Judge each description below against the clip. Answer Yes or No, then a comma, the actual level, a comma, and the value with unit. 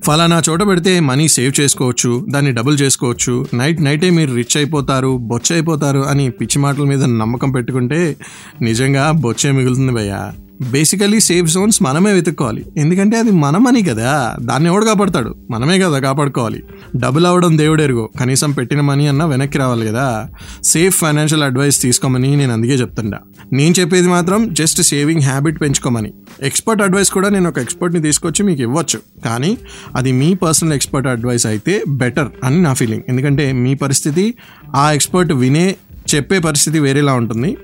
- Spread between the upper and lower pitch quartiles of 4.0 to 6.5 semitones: Yes, average, 4.8 semitones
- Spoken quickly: Yes, fast, 150 wpm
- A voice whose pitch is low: No, medium, 145 Hz